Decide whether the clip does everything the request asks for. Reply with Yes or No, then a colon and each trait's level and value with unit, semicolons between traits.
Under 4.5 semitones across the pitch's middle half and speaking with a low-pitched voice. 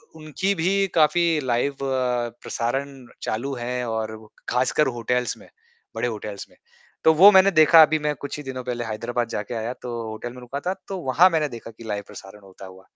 No: average, 4.8 semitones; low, 125 Hz